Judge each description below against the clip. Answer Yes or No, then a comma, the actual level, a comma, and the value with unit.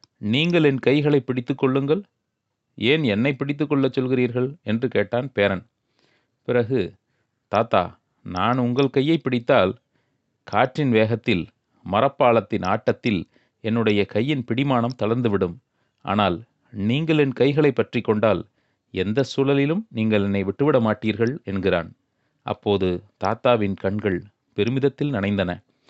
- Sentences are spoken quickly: No, average, 105 wpm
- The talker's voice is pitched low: Yes, low, 120 Hz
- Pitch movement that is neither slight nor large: Yes, average, 4.7 semitones